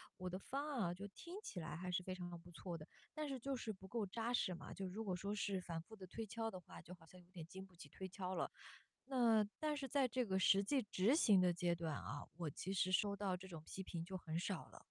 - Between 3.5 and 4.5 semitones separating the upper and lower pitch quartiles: Yes, average, 4.0 semitones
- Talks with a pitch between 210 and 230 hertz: No, high, 190 Hz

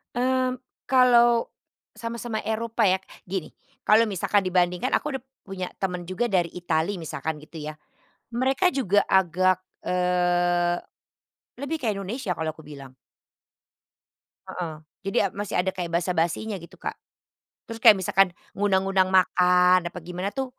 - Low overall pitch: No, high, 190 Hz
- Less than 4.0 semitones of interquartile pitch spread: No, average, 4.4 semitones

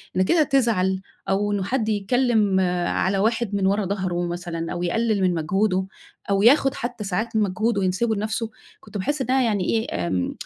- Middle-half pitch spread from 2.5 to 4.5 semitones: Yes, average, 3.5 semitones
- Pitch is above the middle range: Yes, high, 205 Hz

